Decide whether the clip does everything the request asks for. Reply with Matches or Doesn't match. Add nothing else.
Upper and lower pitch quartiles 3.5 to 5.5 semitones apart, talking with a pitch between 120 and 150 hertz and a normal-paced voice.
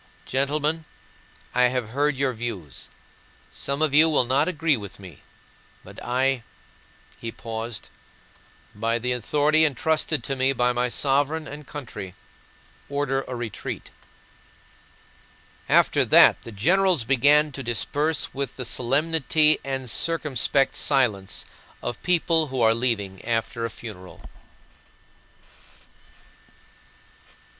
Doesn't match